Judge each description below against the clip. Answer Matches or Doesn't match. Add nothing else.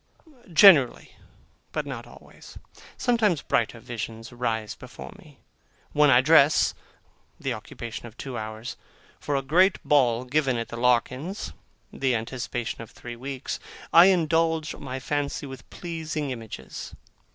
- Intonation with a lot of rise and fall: Doesn't match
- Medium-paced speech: Doesn't match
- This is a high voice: Doesn't match